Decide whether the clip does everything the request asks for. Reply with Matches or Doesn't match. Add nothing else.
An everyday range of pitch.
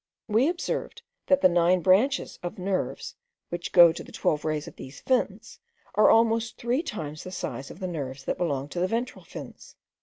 Doesn't match